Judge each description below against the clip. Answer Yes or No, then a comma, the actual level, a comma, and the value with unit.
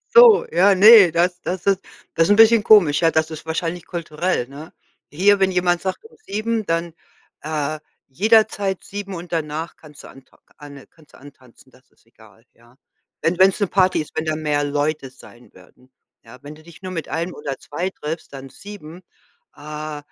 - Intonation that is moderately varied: Yes, average, 4.4 semitones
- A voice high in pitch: No, medium, 165 Hz